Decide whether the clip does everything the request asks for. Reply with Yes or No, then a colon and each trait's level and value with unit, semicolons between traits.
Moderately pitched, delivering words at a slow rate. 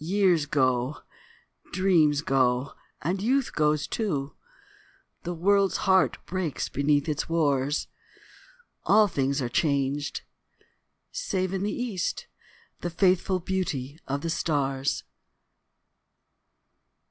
Yes: medium, 160 Hz; slow, 100 wpm